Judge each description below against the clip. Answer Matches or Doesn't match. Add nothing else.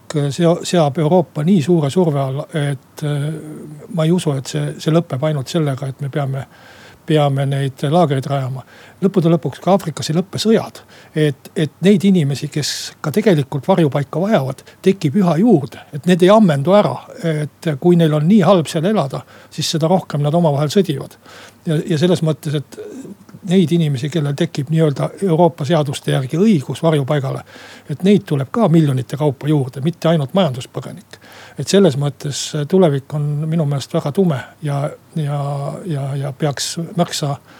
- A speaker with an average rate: Doesn't match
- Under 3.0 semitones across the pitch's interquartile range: Doesn't match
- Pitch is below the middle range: Doesn't match